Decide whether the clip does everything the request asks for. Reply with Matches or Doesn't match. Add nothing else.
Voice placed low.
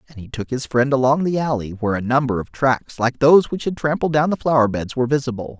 Matches